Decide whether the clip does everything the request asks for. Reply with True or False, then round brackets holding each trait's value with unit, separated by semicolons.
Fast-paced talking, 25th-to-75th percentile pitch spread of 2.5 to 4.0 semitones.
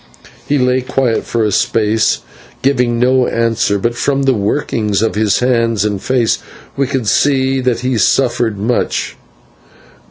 False (150 wpm; 2.9 semitones)